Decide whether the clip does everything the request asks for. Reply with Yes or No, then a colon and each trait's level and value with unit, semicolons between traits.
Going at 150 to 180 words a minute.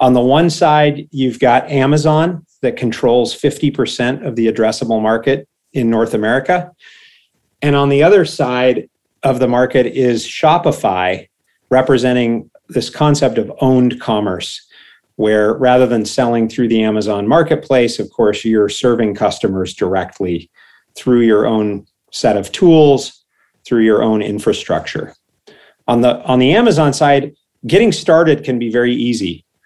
No: average, 140 wpm